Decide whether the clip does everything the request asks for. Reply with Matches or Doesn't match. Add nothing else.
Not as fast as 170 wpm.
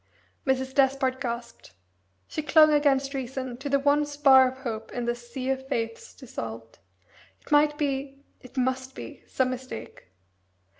Matches